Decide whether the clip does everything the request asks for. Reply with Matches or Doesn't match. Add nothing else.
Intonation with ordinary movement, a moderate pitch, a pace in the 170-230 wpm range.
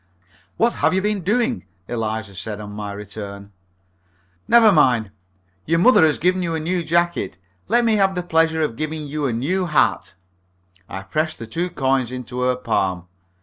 Doesn't match